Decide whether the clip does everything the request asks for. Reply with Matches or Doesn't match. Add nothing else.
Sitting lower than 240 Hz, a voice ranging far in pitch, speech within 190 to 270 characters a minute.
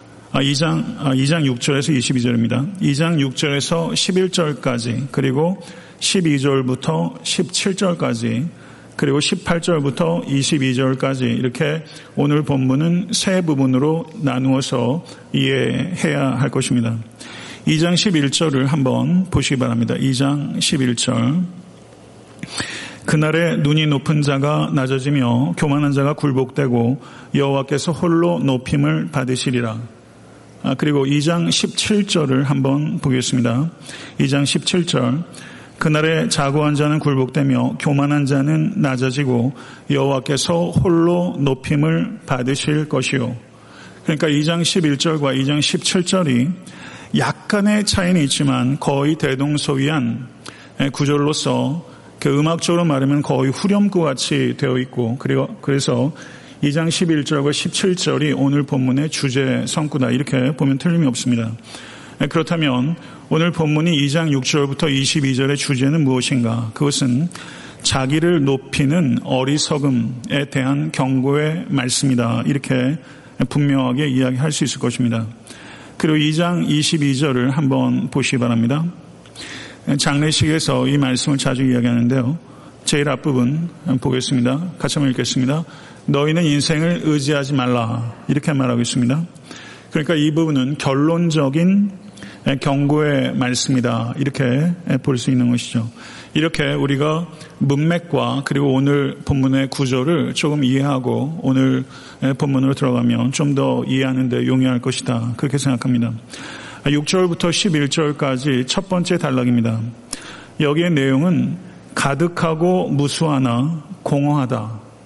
Doesn't match